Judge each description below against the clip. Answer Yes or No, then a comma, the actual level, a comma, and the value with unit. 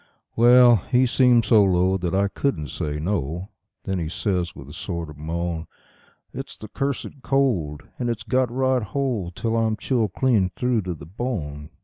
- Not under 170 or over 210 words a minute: Yes, average, 175 wpm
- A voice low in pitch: Yes, low, 100 Hz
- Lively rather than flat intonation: Yes, wide, 6.3 semitones